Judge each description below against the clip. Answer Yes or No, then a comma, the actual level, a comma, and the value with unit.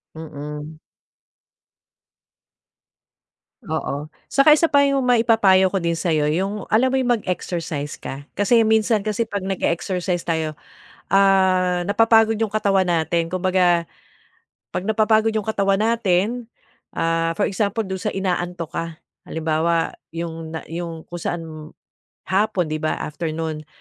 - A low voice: No, medium, 185 Hz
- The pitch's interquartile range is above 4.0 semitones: Yes, average, 4.6 semitones